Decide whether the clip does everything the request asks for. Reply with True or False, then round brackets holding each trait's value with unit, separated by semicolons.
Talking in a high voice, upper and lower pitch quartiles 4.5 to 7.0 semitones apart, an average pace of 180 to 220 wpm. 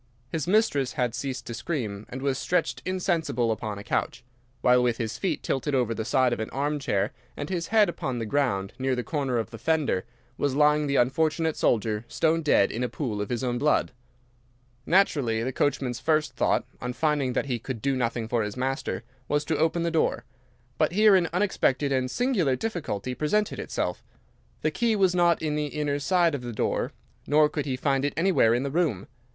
False (140 Hz; 4.8 semitones; 200 wpm)